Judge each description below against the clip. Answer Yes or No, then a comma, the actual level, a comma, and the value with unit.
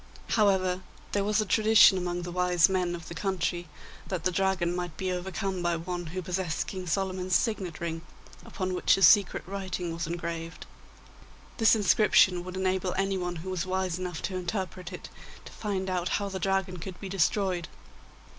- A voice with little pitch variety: Yes, narrow, 1.6 semitones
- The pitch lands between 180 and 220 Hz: Yes, medium, 185 Hz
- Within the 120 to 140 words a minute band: No, average, 175 wpm